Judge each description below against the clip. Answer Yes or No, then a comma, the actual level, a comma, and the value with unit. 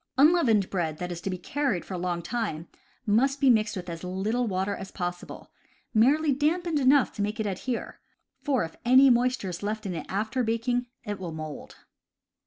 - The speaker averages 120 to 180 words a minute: No, average, 195 wpm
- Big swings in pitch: Yes, wide, 5.9 semitones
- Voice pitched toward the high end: Yes, high, 215 Hz